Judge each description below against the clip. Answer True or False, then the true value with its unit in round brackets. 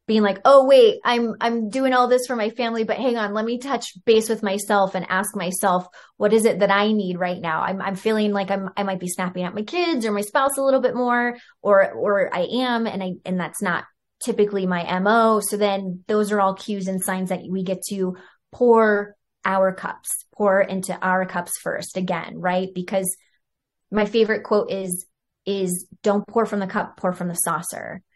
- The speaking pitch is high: True (200 Hz)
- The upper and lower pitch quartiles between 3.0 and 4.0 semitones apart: True (3.3 semitones)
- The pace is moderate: False (215 wpm)